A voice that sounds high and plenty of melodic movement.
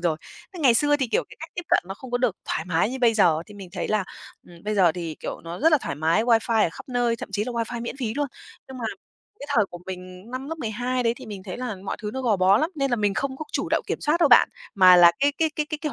Yes: high, 230 Hz; wide, 5.8 semitones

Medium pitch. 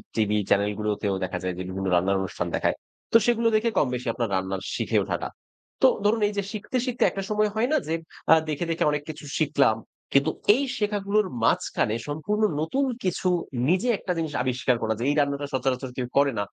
Yes: medium, 145 Hz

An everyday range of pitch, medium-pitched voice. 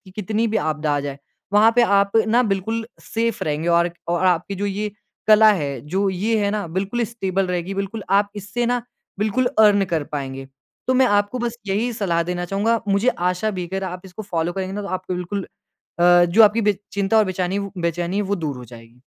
No: average, 3.4 semitones; high, 195 Hz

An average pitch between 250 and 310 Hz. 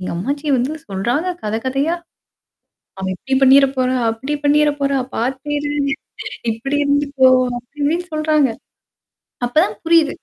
Yes: very high, 275 Hz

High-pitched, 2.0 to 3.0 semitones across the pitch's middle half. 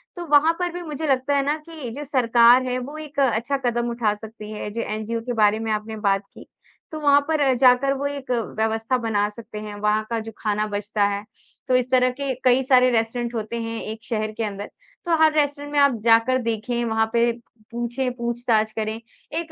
No: high, 235 Hz; average, 3.8 semitones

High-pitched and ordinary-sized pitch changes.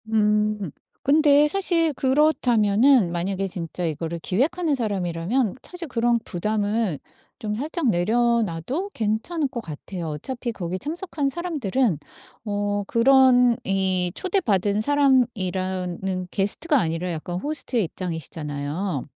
No: high, 215 Hz; wide, 6.7 semitones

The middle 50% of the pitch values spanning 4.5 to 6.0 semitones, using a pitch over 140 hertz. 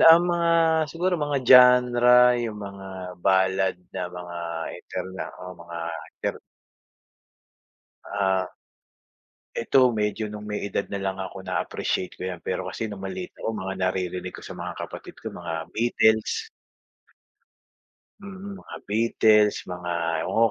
No: average, 4.8 semitones; low, 100 Hz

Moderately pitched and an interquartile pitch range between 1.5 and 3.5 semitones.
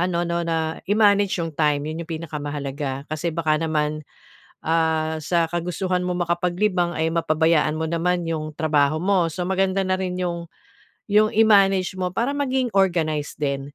Yes: medium, 170 Hz; average, 2.8 semitones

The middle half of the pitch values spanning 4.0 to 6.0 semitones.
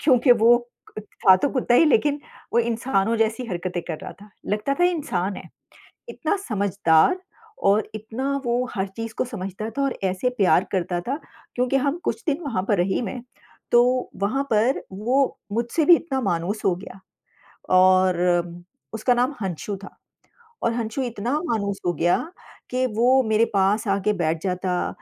Yes: average, 4.8 semitones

